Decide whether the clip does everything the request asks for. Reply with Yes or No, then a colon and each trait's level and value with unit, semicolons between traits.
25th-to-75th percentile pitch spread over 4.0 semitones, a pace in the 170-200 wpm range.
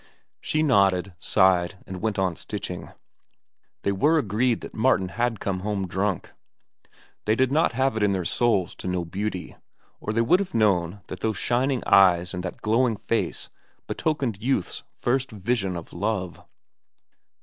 No: average, 4.4 semitones; average, 160 wpm